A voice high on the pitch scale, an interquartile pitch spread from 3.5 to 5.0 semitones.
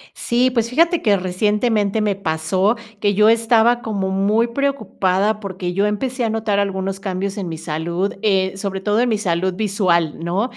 No: high, 200 Hz; average, 2.9 semitones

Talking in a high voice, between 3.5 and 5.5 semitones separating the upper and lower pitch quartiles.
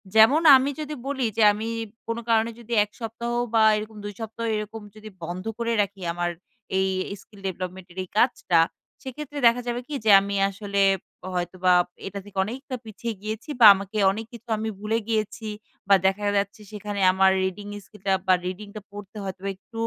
No: high, 210 Hz; average, 2.8 semitones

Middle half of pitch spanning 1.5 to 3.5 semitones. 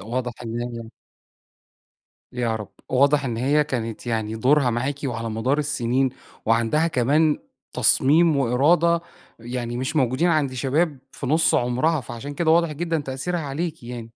No: average, 4.1 semitones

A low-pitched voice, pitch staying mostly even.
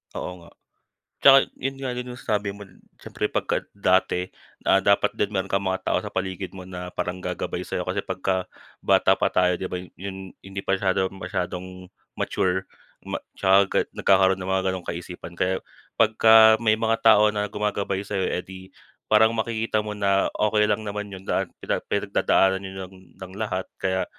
Yes: very low, 95 Hz; narrow, 2.1 semitones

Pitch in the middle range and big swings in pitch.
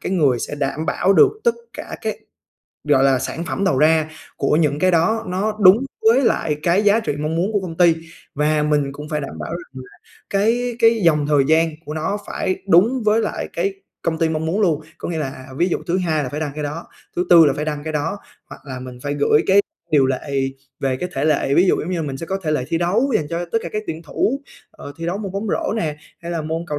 No: medium, 165 Hz; average, 4.3 semitones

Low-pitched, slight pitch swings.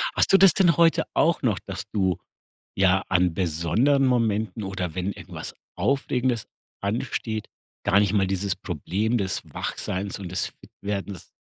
No: low, 100 Hz; average, 4.2 semitones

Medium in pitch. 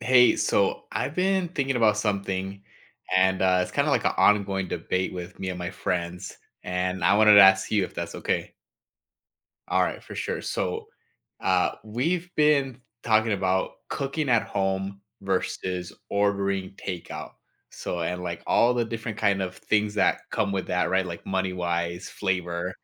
No: very low, 95 Hz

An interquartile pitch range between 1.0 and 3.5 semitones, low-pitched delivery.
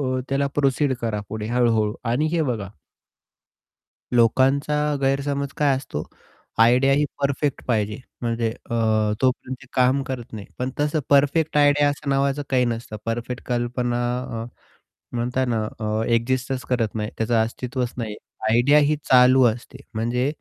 Yes: average, 3.1 semitones; low, 125 Hz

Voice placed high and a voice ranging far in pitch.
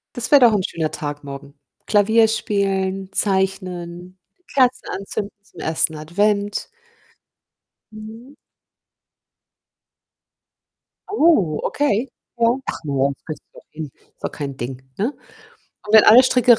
Yes: high, 195 Hz; wide, 5.9 semitones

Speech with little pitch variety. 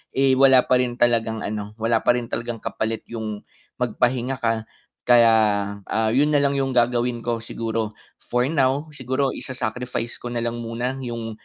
Yes: narrow, 2.1 semitones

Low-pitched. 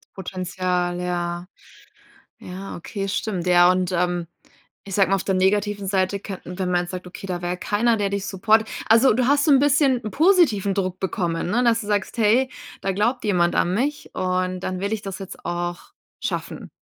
No: high, 195 Hz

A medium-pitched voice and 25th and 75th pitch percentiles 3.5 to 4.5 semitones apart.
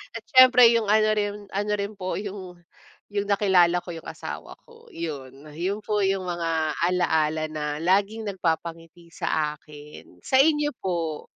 Yes: medium, 180 Hz; average, 4.2 semitones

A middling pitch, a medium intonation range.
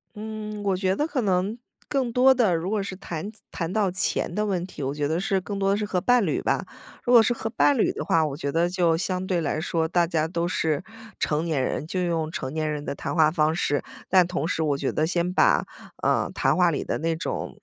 Yes: medium, 180 Hz; average, 4.2 semitones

